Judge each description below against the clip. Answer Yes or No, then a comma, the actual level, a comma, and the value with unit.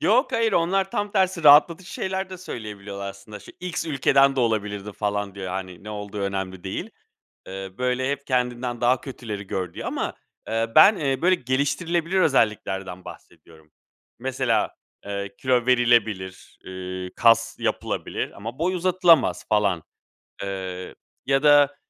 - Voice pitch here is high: No, low, 120 Hz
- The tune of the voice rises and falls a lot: Yes, wide, 7.2 semitones